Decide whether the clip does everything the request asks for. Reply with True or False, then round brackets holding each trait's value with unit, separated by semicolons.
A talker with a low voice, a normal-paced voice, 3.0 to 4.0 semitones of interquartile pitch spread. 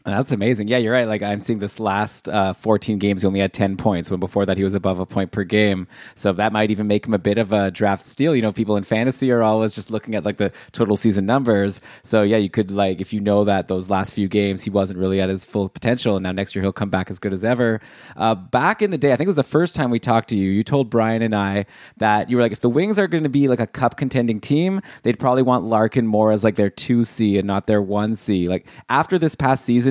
False (105 Hz; 285 wpm; 3.3 semitones)